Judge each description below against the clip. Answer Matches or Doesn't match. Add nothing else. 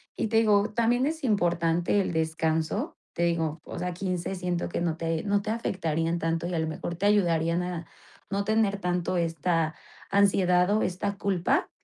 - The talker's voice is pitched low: Doesn't match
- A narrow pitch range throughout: Doesn't match